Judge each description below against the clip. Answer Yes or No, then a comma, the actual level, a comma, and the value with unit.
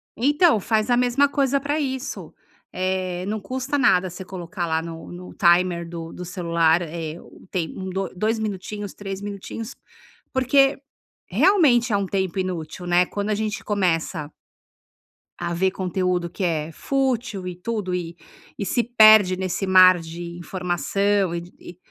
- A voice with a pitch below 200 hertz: Yes, high, 190 Hz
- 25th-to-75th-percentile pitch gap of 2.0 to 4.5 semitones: Yes, average, 4.0 semitones